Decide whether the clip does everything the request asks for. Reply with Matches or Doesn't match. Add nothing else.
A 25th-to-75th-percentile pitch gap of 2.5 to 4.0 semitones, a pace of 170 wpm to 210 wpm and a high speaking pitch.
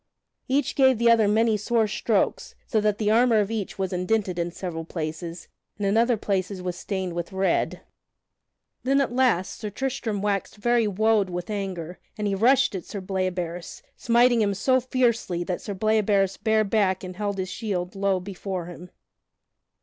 Matches